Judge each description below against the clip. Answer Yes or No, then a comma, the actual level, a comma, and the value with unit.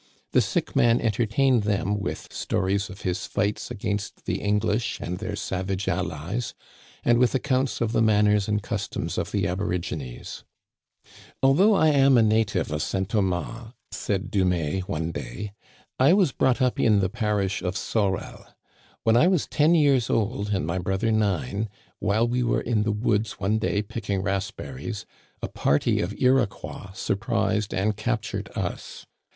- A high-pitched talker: No, low, 105 Hz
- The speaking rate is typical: Yes, average, 160 wpm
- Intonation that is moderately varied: Yes, average, 3.5 semitones